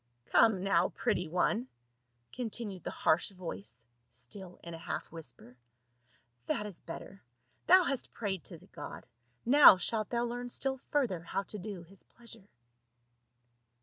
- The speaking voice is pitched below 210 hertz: Yes, high, 190 Hz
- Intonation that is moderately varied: No, wide, 5.9 semitones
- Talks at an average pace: Yes, average, 150 wpm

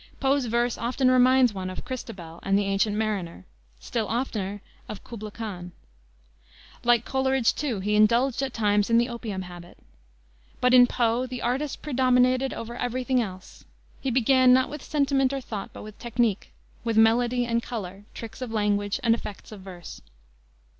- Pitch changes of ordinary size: Yes, average, 3.7 semitones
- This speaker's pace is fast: No, average, 165 wpm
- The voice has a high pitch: Yes, high, 235 Hz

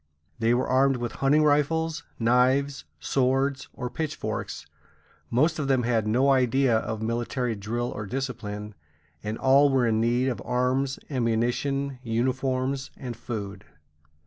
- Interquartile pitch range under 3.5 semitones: Yes, average, 2.8 semitones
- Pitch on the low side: Yes, low, 125 Hz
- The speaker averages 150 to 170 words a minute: No, slow, 135 wpm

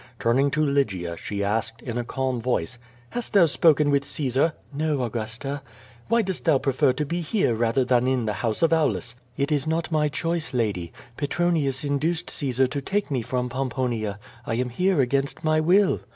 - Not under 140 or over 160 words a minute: No, average, 185 wpm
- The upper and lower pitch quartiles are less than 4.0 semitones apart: No, average, 4.5 semitones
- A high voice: No, low, 135 Hz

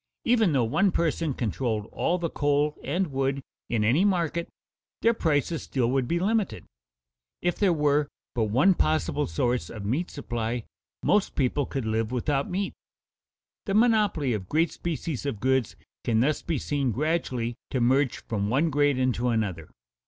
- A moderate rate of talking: Yes, average, 160 wpm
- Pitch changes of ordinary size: No, wide, 5.8 semitones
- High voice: No, medium, 140 Hz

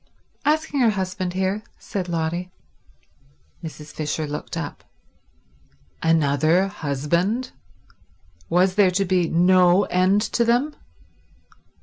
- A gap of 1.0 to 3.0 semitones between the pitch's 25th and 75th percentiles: No, average, 3.8 semitones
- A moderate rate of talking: No, slow, 100 wpm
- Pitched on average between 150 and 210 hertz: Yes, medium, 185 Hz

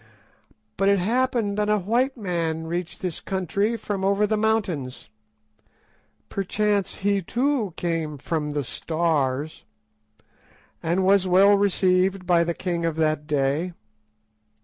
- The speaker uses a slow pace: Yes, slow, 120 wpm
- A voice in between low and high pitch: Yes, medium, 180 Hz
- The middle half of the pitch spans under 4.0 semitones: No, average, 4.6 semitones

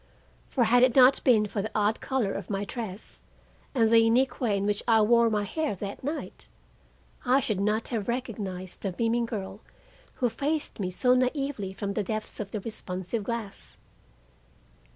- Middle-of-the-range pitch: No, high, 220 Hz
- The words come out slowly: No, average, 175 wpm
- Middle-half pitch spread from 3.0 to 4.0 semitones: Yes, average, 3.5 semitones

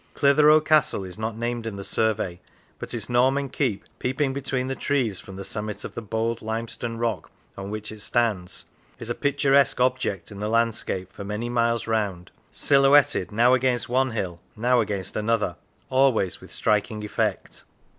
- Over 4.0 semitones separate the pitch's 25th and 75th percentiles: No, average, 3.6 semitones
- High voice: No, low, 115 Hz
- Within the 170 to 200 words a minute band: Yes, average, 175 wpm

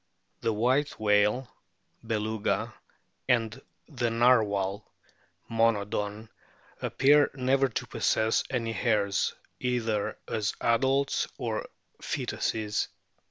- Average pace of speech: No, slow, 85 wpm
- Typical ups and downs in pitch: Yes, average, 3.0 semitones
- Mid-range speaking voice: No, low, 115 Hz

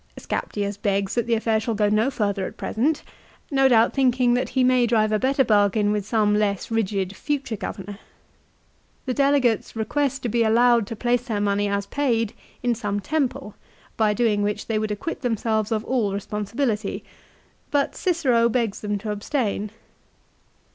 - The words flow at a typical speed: Yes, average, 170 wpm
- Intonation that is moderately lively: Yes, average, 3.1 semitones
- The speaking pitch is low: No, high, 225 Hz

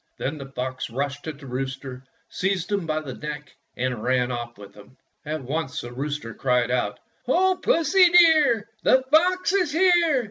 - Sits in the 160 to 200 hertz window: No, medium, 145 Hz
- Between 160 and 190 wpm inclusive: Yes, average, 180 wpm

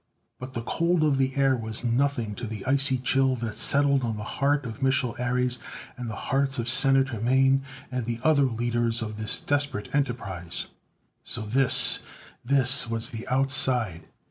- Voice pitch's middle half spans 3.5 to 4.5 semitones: No, average, 2.8 semitones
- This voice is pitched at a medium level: No, low, 125 Hz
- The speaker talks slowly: No, average, 170 wpm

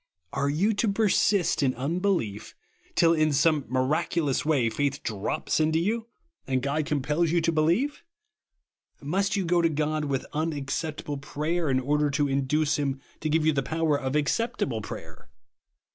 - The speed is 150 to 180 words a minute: Yes, average, 165 wpm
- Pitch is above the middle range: No, medium, 150 Hz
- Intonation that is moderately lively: Yes, average, 3.2 semitones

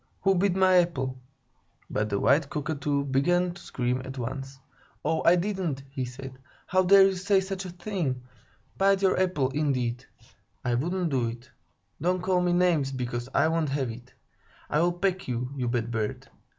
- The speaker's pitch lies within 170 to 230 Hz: No, medium, 145 Hz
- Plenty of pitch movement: Yes, wide, 6.0 semitones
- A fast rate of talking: No, average, 175 wpm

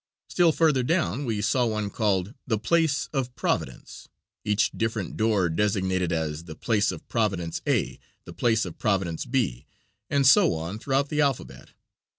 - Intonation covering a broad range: Yes, wide, 6.1 semitones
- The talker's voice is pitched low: Yes, low, 110 Hz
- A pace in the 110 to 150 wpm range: No, average, 160 wpm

